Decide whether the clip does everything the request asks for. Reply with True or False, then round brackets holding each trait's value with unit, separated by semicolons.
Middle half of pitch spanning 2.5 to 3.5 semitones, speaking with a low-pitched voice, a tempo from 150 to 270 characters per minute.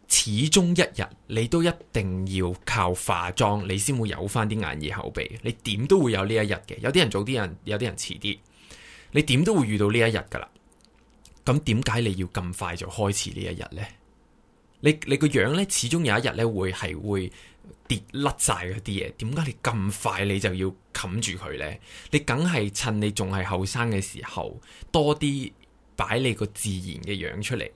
False (5.2 semitones; 110 Hz; 265 characters per minute)